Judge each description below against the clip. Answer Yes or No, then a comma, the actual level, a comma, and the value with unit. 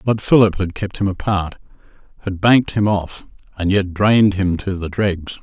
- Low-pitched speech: Yes, very low, 95 Hz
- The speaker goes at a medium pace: Yes, average, 190 wpm